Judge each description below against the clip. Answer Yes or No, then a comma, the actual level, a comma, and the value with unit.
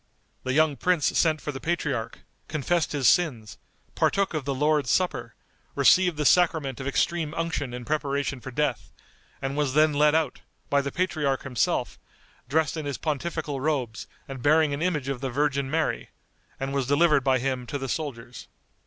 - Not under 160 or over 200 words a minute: Yes, average, 175 wpm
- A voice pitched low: No, medium, 145 Hz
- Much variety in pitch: No, average, 2.9 semitones